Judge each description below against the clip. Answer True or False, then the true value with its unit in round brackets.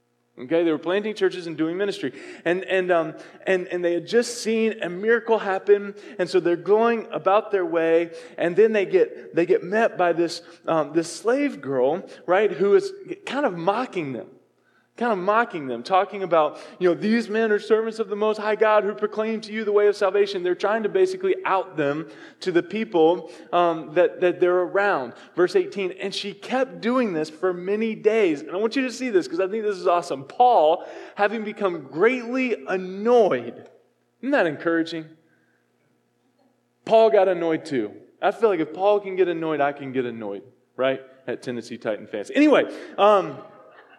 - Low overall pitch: False (195 Hz)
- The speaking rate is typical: True (190 wpm)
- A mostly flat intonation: False (4.9 semitones)